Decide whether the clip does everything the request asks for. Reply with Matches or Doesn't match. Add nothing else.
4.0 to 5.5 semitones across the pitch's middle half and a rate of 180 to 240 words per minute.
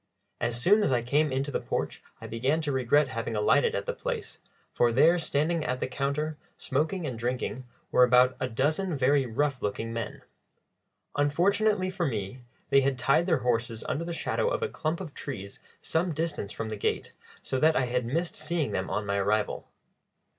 Matches